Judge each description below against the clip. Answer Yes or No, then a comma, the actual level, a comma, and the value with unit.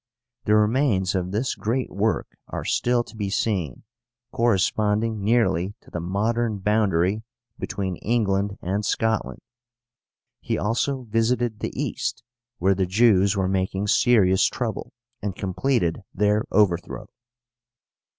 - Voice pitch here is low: Yes, low, 105 Hz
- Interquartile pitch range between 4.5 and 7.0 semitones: No, average, 3.0 semitones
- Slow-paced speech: Yes, slow, 120 wpm